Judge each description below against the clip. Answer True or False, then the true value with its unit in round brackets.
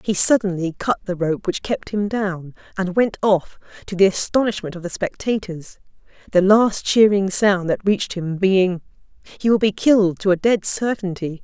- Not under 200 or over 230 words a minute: False (175 wpm)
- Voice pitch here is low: False (195 Hz)